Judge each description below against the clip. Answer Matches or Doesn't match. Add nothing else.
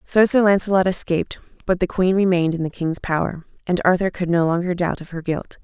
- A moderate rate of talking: Doesn't match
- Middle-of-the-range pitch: Matches